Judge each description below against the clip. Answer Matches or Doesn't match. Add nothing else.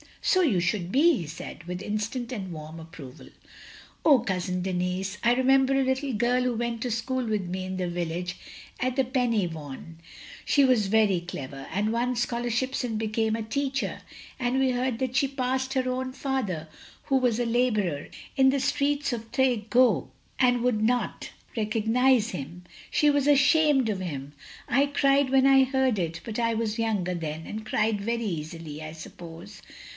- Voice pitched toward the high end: Matches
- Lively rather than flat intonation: Matches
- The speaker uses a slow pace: Doesn't match